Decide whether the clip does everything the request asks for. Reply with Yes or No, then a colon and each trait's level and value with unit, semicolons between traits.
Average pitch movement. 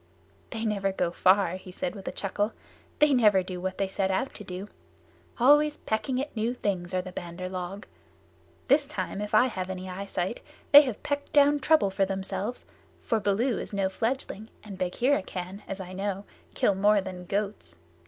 Yes: average, 3.9 semitones